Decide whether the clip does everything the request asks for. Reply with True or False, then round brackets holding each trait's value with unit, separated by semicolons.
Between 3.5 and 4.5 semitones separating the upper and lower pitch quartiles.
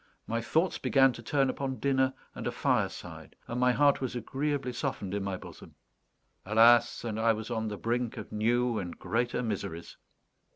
False (3.0 semitones)